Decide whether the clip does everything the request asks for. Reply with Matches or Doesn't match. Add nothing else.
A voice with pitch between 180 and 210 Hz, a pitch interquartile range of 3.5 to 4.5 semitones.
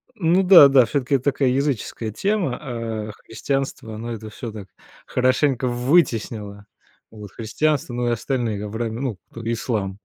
Doesn't match